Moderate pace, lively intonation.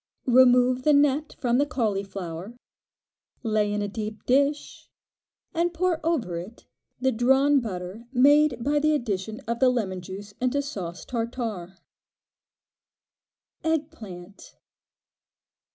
No: slow, 120 wpm; wide, 5.8 semitones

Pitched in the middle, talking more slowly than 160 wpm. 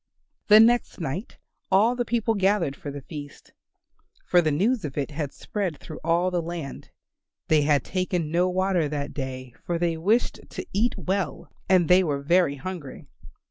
No: medium, 175 Hz; average, 175 wpm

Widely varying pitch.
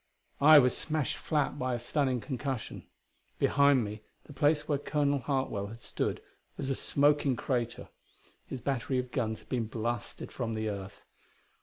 No: average, 3.7 semitones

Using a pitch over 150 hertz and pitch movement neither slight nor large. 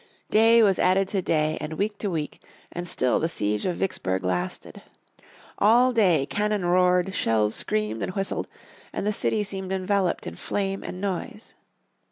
Yes: medium, 185 Hz; average, 4.9 semitones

